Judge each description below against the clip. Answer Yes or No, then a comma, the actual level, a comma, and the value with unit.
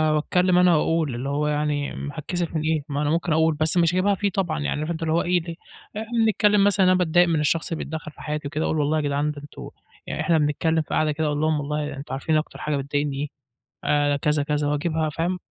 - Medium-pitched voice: Yes, medium, 155 Hz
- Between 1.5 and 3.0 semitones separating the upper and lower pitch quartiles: Yes, narrow, 2.4 semitones